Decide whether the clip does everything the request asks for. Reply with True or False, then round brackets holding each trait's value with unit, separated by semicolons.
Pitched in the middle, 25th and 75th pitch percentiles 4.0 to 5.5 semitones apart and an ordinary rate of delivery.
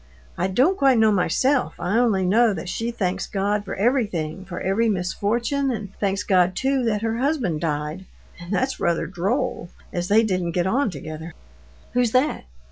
False (200 Hz; 5.0 semitones; 175 wpm)